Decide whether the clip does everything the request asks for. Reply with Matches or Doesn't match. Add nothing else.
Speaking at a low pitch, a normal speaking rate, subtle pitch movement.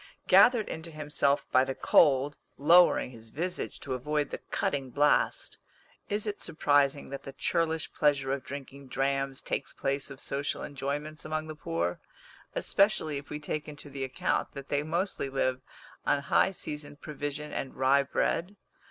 Doesn't match